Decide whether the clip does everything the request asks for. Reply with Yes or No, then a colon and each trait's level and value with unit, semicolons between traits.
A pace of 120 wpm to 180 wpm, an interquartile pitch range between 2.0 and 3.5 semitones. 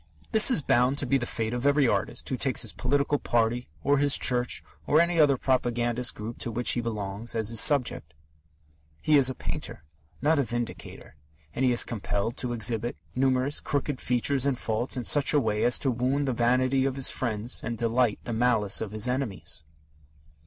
No: average, 195 wpm; average, 2.9 semitones